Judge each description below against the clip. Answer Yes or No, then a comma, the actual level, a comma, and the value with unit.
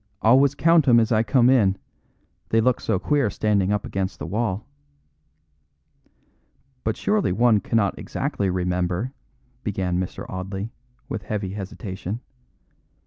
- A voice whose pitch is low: Yes, low, 105 Hz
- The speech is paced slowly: Yes, slow, 130 wpm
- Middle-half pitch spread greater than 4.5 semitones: No, average, 3.8 semitones